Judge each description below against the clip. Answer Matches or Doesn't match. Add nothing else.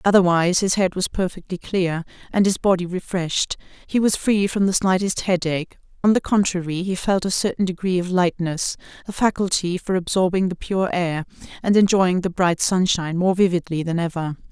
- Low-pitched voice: Doesn't match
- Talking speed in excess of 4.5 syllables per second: Matches